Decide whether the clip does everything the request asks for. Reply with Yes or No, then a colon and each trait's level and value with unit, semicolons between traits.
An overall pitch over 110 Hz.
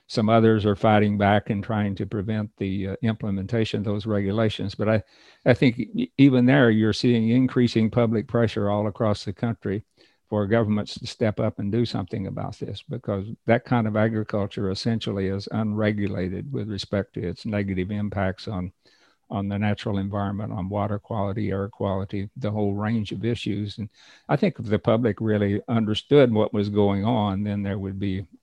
No: low, 105 Hz